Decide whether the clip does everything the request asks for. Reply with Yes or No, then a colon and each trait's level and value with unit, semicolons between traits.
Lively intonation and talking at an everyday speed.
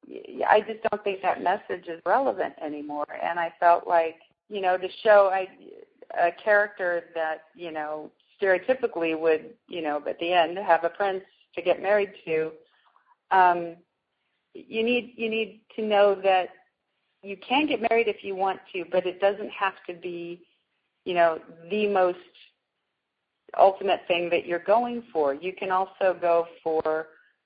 No: average, 3.5 semitones; average, 160 wpm